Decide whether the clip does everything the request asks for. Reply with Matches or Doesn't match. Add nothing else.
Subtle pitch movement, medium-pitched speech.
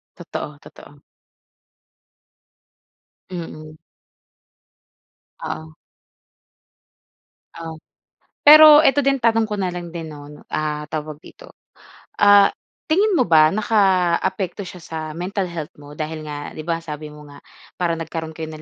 Doesn't match